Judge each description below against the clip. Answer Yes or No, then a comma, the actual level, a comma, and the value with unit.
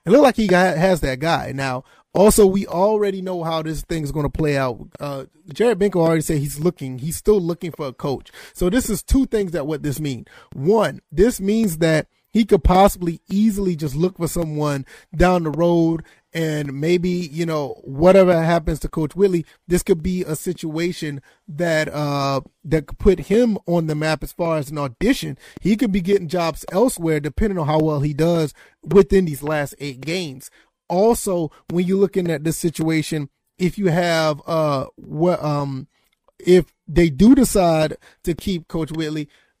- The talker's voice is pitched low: No, medium, 165 Hz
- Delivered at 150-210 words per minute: Yes, average, 190 wpm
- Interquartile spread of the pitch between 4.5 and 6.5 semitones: No, average, 3.6 semitones